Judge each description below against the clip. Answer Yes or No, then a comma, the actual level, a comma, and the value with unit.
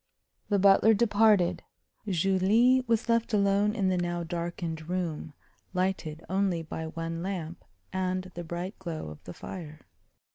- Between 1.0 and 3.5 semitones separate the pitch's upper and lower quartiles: Yes, average, 3.1 semitones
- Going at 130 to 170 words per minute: Yes, average, 140 wpm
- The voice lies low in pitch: No, medium, 185 Hz